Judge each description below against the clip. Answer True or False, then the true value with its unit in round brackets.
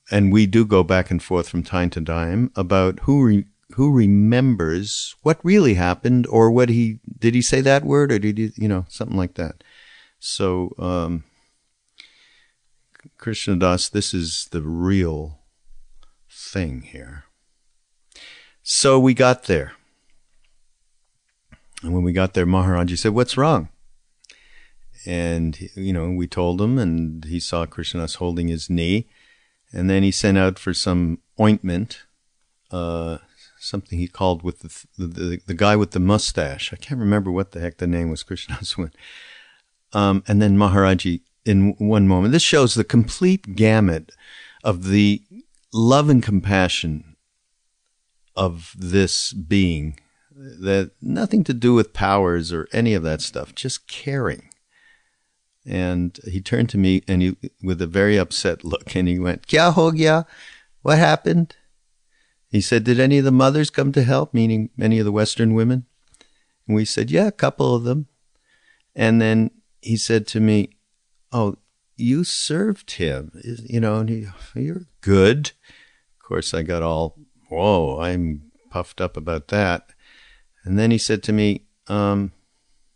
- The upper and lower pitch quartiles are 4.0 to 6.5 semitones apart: True (5.1 semitones)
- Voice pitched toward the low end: True (100 Hz)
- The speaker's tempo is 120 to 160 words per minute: True (155 wpm)